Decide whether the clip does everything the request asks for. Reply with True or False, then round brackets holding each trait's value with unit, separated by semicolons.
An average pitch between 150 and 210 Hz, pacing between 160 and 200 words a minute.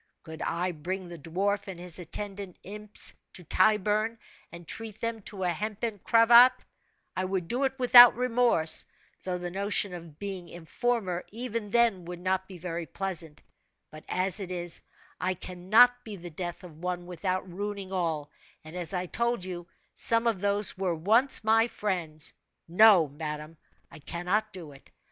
True (185 Hz; 165 wpm)